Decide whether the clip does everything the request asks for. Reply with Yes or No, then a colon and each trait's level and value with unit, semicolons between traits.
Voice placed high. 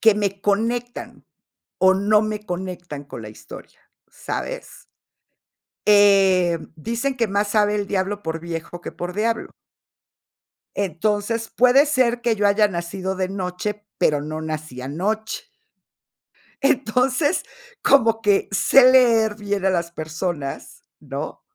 Yes: high, 205 Hz